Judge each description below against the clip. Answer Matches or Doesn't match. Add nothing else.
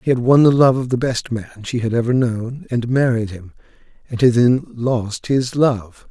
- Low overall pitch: Matches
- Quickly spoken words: Matches